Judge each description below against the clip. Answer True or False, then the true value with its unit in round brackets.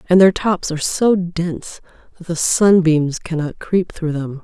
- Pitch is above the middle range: False (170 Hz)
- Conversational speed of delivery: True (175 wpm)